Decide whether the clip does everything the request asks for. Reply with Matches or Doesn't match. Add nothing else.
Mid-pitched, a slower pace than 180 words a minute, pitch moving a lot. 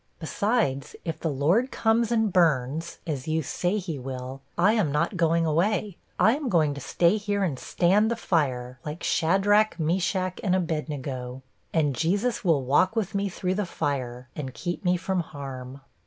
Matches